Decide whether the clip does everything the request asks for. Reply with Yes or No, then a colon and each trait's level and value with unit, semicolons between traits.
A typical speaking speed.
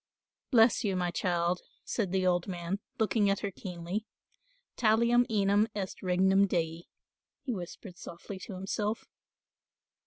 No: slow, 130 wpm